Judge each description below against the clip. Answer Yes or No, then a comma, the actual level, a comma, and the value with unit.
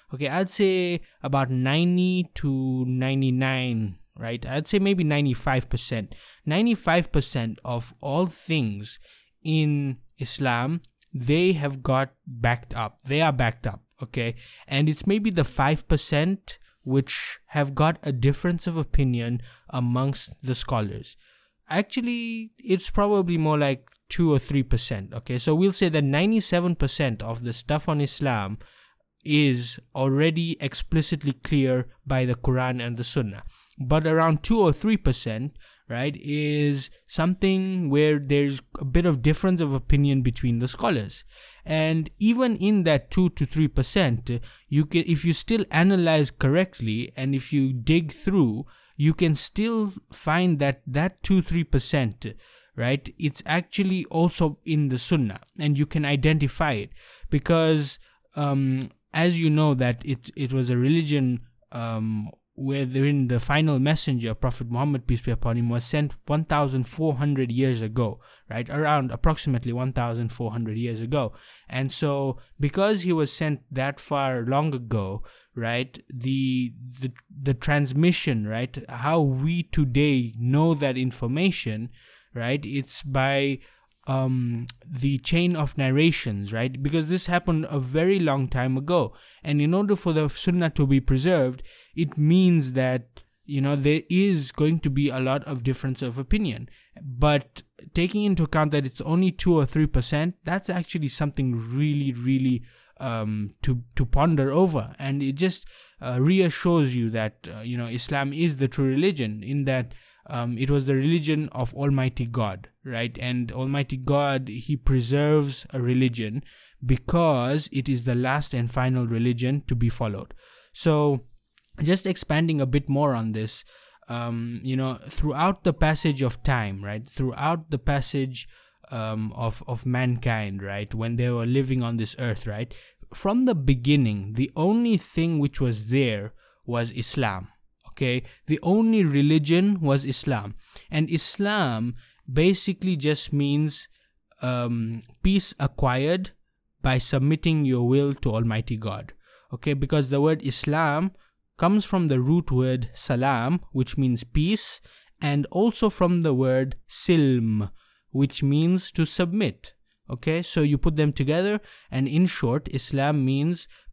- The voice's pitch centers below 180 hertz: Yes, medium, 140 Hz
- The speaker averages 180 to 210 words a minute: No, average, 145 wpm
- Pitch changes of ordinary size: Yes, average, 4.2 semitones